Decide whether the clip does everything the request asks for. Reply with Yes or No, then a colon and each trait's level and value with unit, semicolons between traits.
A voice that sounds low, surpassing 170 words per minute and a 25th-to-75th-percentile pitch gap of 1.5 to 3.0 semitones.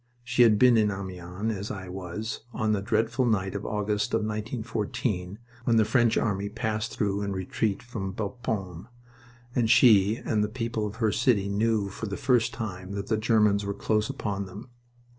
Yes: low, 105 Hz; average, 180 wpm; narrow, 2.4 semitones